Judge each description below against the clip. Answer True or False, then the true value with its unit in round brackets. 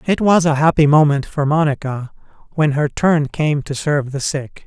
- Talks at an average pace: True (195 wpm)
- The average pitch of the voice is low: False (150 Hz)